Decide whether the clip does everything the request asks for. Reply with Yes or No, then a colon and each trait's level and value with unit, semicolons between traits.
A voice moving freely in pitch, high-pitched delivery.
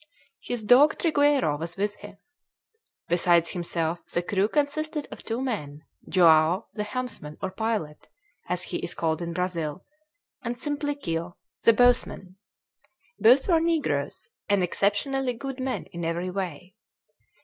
Yes: wide, 7.0 semitones; high, 200 Hz